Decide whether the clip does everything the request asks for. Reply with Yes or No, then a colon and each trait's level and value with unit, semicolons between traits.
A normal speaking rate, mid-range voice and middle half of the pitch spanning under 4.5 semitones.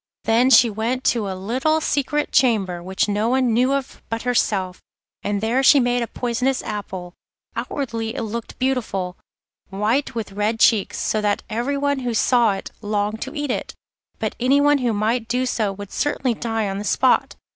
No: average, 180 wpm; high, 230 Hz; average, 3.7 semitones